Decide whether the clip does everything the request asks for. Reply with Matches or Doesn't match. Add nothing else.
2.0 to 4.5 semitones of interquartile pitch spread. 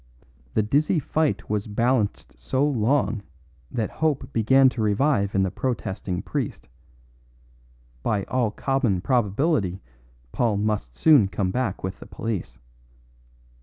Doesn't match